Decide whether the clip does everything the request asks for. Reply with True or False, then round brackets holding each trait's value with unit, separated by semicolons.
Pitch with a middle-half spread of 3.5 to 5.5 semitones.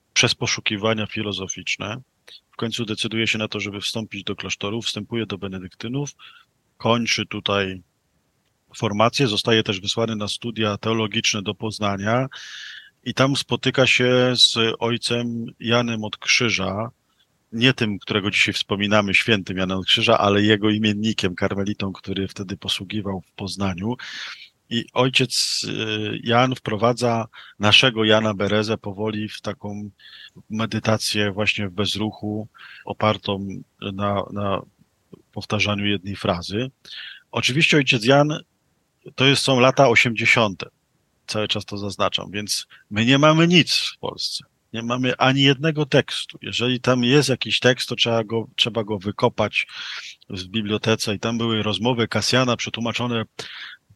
False (2.8 semitones)